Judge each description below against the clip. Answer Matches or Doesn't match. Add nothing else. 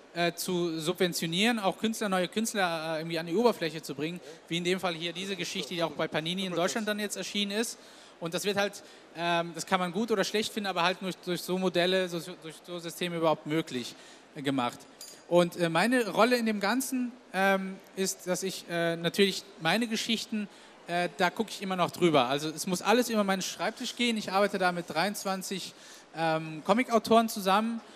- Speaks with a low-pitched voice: Doesn't match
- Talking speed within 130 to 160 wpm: Doesn't match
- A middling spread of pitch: Matches